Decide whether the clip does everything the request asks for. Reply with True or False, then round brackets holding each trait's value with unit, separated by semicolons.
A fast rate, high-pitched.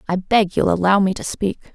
True (240 wpm; 195 Hz)